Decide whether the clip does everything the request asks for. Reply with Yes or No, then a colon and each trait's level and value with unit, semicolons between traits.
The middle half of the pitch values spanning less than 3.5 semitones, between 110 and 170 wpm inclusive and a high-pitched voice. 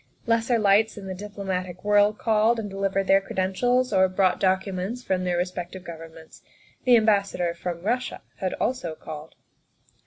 Yes: average, 2.9 semitones; average, 160 wpm; high, 195 Hz